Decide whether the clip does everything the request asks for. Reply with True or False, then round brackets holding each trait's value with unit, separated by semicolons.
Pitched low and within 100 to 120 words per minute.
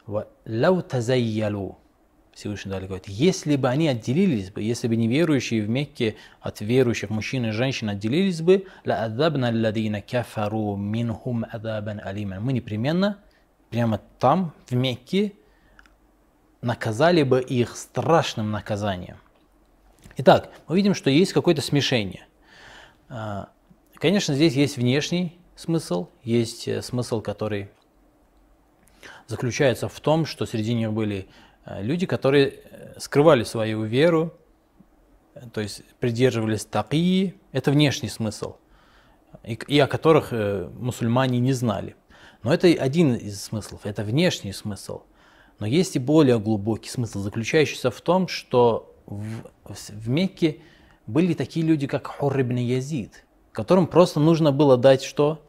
True (125 Hz; 115 wpm)